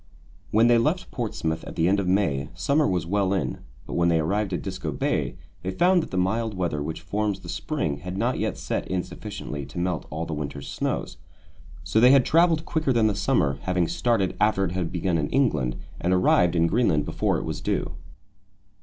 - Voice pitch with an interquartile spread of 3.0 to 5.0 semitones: No, wide, 5.4 semitones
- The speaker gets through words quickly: Yes, fast, 215 wpm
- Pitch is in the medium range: No, very low, 95 Hz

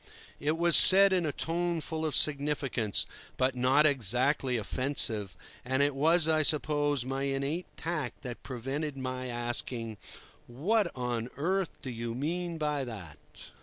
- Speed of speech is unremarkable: Yes, average, 145 wpm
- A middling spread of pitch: Yes, average, 4.3 semitones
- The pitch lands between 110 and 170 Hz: Yes, medium, 140 Hz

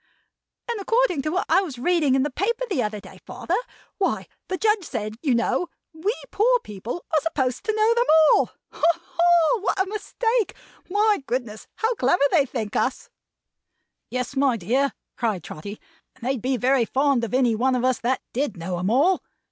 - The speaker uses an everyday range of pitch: No, wide, 7.6 semitones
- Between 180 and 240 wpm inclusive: Yes, average, 195 wpm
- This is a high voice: Yes, very high, 275 Hz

